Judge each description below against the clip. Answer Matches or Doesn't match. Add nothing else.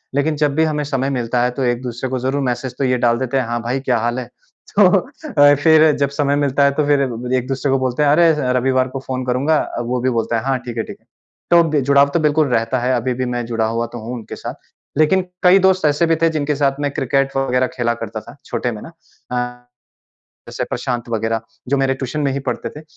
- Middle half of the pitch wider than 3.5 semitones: Doesn't match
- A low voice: Matches